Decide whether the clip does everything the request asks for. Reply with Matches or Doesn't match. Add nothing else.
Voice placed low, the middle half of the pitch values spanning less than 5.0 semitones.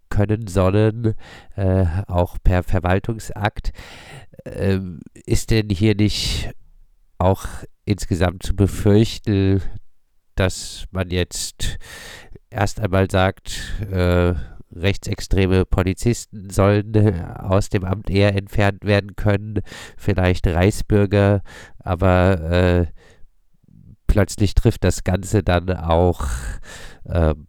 Matches